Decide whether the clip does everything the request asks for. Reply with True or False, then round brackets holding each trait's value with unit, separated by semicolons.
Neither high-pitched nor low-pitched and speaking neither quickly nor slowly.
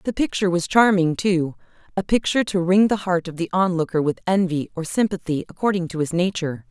True (180 Hz; 190 wpm)